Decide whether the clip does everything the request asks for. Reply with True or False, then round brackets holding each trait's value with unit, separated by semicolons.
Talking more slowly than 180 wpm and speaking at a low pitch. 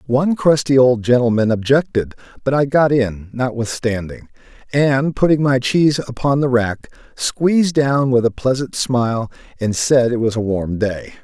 True (160 wpm; 125 Hz)